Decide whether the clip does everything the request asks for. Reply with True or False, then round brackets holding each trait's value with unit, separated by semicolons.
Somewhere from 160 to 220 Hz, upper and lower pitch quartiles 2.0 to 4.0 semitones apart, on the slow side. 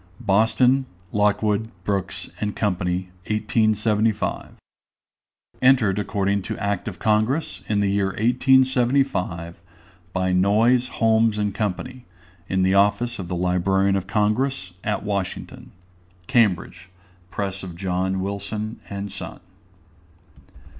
False (100 Hz; 2.9 semitones; 110 wpm)